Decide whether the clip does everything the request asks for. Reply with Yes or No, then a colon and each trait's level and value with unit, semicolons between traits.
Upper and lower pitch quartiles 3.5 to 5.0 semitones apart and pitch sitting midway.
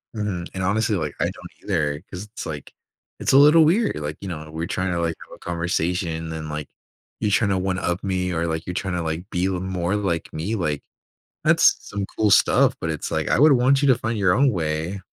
No: average, 4.1 semitones; very low, 90 Hz